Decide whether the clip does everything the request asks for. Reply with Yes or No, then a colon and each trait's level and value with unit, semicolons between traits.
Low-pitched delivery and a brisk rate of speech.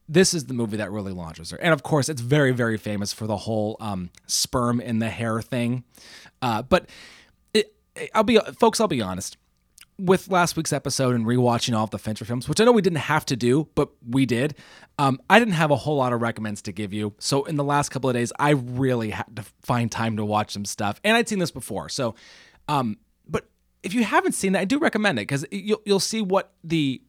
Yes: low, 130 Hz; fast, 235 wpm